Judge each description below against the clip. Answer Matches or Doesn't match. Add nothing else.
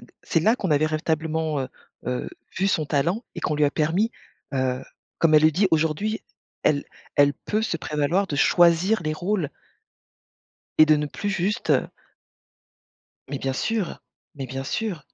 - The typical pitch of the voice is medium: Matches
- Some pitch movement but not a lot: Matches